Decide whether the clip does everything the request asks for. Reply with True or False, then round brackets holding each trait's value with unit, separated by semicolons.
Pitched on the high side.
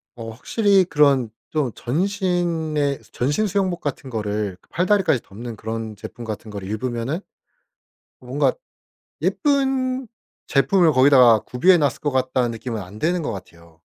False (130 Hz)